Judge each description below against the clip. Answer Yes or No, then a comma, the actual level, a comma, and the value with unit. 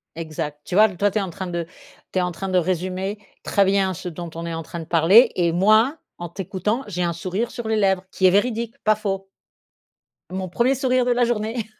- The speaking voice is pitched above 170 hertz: Yes, high, 190 Hz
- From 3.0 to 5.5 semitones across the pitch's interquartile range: Yes, average, 3.8 semitones